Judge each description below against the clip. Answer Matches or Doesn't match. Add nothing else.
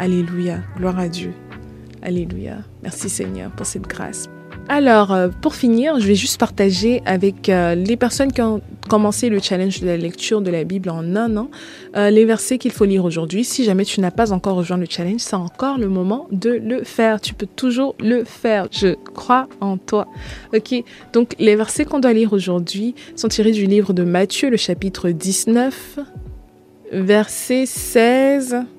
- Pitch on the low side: Doesn't match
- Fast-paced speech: Doesn't match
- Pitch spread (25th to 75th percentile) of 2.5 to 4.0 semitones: Doesn't match